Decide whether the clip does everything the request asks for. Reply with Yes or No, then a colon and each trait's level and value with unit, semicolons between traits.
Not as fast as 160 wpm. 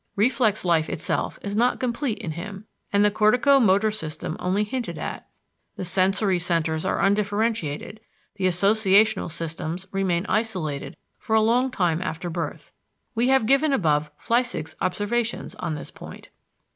Yes: average, 145 wpm